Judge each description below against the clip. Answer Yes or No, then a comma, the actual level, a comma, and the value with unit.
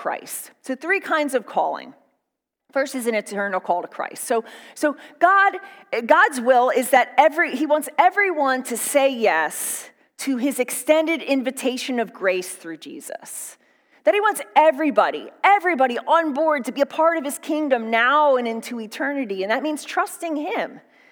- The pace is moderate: Yes, average, 165 wpm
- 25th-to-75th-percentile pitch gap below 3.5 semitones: No, average, 4.2 semitones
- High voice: Yes, very high, 275 Hz